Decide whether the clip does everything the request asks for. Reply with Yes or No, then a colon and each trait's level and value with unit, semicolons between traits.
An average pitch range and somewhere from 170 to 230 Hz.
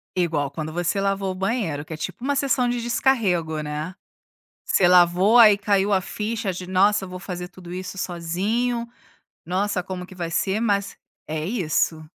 Yes: average, 3.3 semitones; medium, 185 Hz